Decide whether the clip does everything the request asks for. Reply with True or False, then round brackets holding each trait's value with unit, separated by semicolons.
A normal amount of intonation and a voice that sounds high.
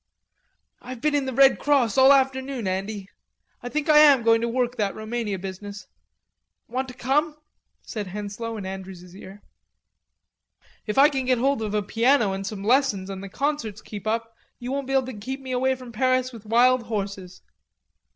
True (4.4 semitones; 235 Hz)